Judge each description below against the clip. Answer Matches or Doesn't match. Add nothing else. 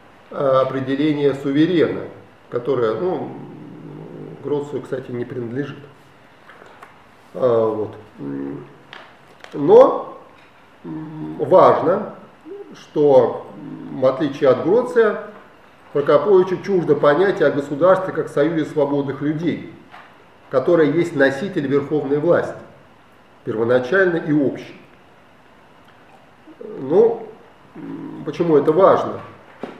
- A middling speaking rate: Doesn't match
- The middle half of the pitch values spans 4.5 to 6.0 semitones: Matches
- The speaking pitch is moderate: Matches